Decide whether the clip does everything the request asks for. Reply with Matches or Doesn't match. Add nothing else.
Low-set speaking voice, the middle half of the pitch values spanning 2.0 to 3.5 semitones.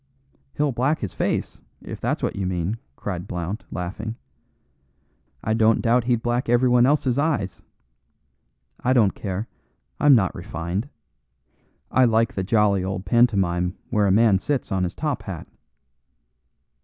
Doesn't match